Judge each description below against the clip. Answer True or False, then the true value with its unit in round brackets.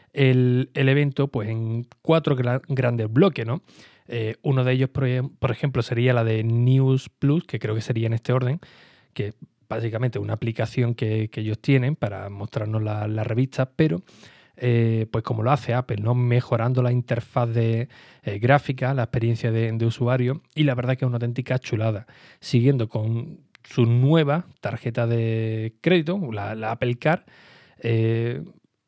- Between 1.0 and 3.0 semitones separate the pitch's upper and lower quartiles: True (2.7 semitones)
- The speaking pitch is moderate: False (125 Hz)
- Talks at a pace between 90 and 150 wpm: False (170 wpm)